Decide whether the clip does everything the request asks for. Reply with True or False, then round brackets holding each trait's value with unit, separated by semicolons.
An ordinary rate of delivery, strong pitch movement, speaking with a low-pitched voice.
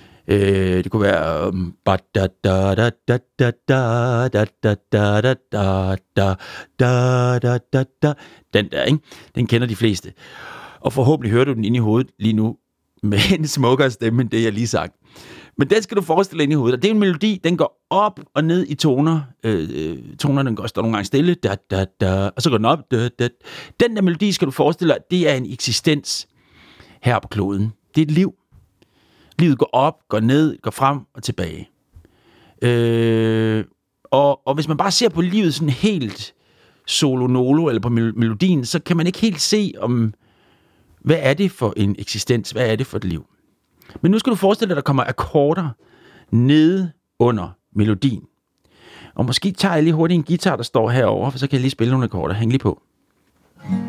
True (175 wpm; 6.0 semitones; 125 Hz)